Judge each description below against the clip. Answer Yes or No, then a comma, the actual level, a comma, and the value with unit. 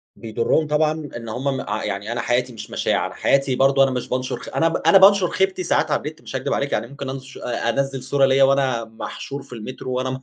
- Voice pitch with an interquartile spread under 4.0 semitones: Yes, narrow, 2.4 semitones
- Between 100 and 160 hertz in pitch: Yes, low, 135 Hz